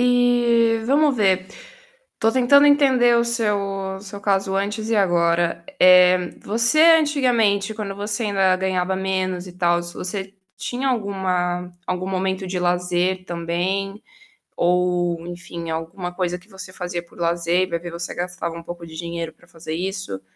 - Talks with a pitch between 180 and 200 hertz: Yes, medium, 185 Hz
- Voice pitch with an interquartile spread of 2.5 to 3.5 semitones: Yes, average, 3.0 semitones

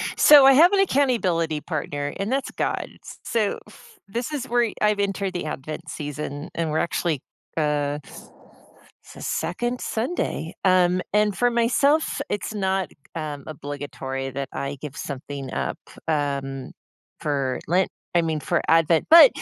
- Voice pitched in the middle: Yes, medium, 170 Hz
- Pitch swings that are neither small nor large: No, wide, 8.0 semitones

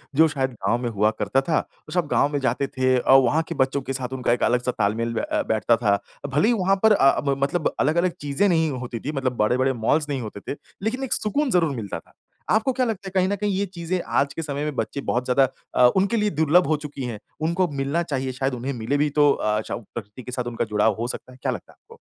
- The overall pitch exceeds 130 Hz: Yes, medium, 140 Hz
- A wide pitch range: Yes, wide, 5.7 semitones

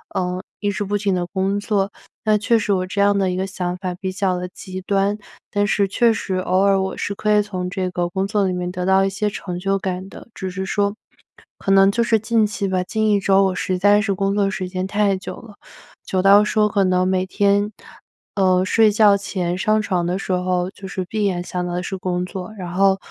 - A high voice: Yes, high, 195 Hz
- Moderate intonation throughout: No, narrow, 1.8 semitones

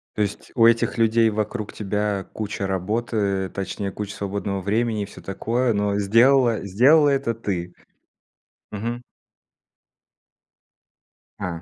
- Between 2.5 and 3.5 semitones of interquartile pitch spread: Yes, average, 2.8 semitones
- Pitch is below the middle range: Yes, low, 105 Hz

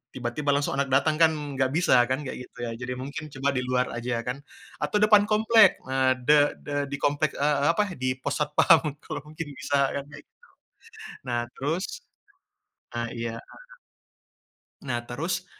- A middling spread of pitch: Yes, average, 3.3 semitones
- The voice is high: No, medium, 140 Hz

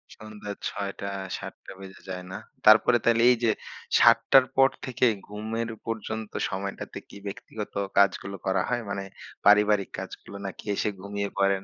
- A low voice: Yes, low, 105 Hz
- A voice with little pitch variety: Yes, narrow, 2.1 semitones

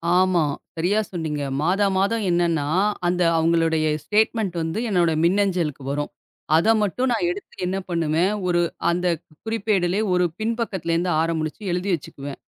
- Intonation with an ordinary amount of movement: Yes, average, 3.5 semitones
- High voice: No, medium, 175 Hz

